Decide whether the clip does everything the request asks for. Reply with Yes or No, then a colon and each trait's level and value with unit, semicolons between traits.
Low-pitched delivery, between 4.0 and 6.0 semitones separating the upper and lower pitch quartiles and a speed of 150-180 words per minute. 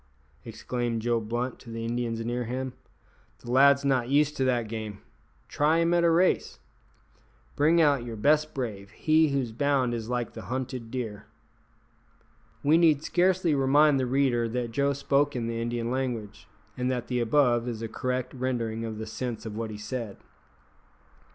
No: low, 125 Hz; average, 3.4 semitones; average, 170 wpm